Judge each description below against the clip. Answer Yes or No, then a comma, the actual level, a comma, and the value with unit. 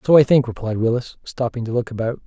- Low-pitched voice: Yes, low, 120 Hz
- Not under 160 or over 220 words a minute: No, fast, 240 wpm